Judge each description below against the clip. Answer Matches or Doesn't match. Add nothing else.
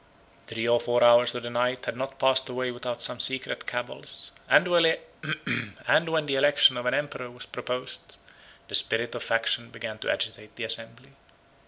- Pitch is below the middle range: Matches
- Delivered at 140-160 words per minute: Doesn't match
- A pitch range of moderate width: Doesn't match